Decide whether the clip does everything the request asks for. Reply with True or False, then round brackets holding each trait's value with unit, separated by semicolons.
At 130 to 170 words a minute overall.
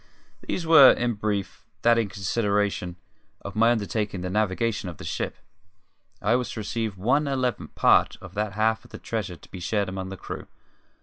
False (185 wpm)